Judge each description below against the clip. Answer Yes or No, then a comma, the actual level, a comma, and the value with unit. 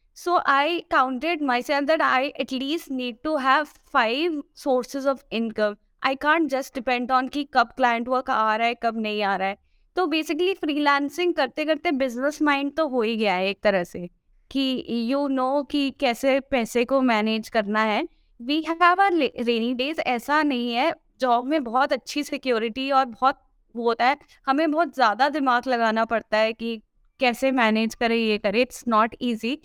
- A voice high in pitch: Yes, very high, 260 Hz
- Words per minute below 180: No, fast, 190 wpm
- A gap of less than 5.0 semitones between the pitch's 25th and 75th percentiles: Yes, average, 3.9 semitones